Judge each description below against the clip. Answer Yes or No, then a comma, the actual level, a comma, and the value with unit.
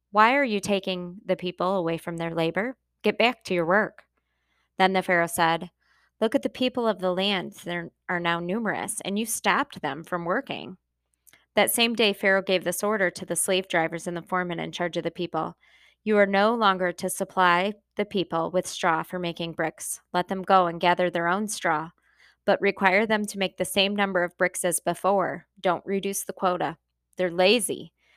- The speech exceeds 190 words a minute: Yes, average, 200 wpm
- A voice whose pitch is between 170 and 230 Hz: Yes, medium, 185 Hz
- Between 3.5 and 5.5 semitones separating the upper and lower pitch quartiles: No, narrow, 2.6 semitones